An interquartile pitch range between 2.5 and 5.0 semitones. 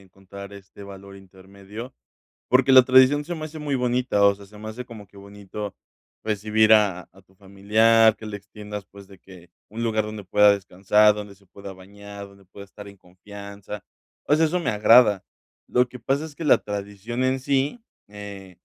Yes: average, 2.8 semitones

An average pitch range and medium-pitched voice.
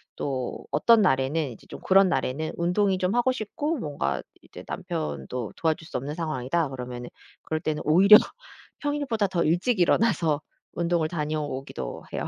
No: wide, 6.2 semitones; medium, 160 Hz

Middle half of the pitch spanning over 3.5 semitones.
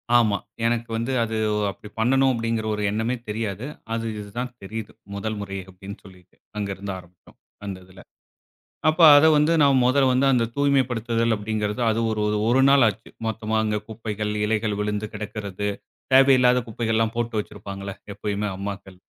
No: average, 2.8 semitones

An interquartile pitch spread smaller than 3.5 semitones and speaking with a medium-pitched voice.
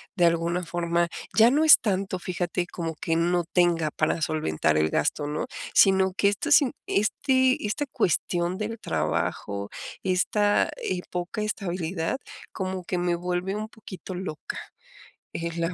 Yes: average, 2.9 semitones; medium, 180 Hz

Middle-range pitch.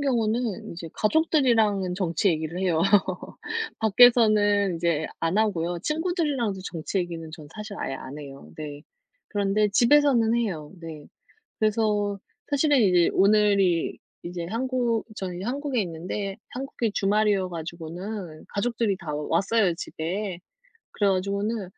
No: high, 200 Hz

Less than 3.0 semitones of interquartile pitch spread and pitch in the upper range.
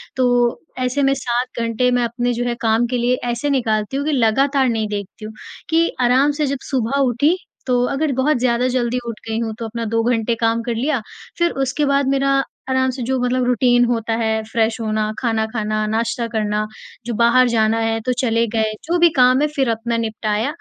Yes: narrow, 2.5 semitones; high, 240 Hz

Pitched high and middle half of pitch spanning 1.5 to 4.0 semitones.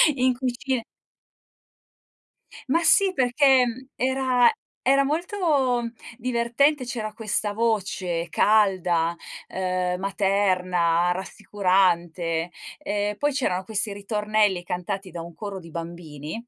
No: high, 205 Hz; wide, 5.8 semitones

